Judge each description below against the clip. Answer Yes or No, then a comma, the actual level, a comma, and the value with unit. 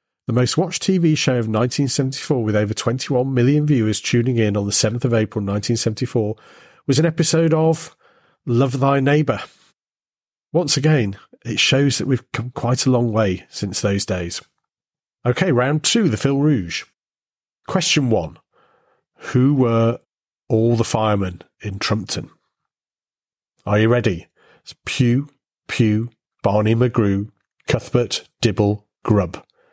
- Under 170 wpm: Yes, average, 145 wpm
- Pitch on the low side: Yes, low, 120 Hz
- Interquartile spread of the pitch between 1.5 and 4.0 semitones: No, average, 4.4 semitones